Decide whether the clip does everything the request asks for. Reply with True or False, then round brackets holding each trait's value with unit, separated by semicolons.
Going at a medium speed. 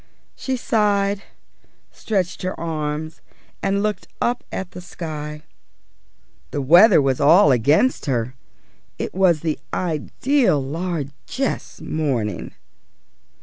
False (105 wpm)